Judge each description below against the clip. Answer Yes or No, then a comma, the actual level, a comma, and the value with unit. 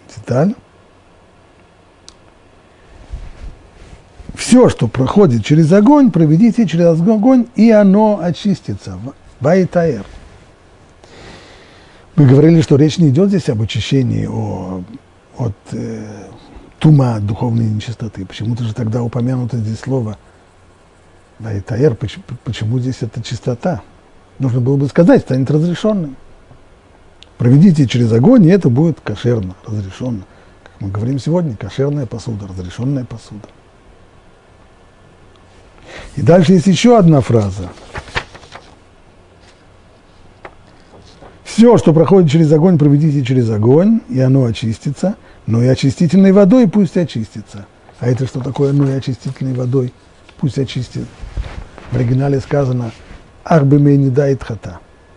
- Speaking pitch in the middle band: No, low, 120 Hz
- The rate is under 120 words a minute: Yes, slow, 110 wpm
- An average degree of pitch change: No, wide, 7.3 semitones